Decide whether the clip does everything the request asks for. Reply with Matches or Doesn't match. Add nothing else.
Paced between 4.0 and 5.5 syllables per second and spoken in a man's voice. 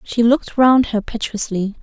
Doesn't match